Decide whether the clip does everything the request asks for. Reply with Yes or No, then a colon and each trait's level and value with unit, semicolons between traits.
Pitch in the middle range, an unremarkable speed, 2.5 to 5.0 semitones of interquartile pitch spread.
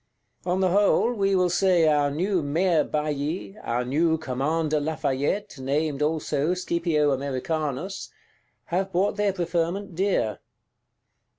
No: medium, 160 Hz; slow, 120 wpm; average, 4.1 semitones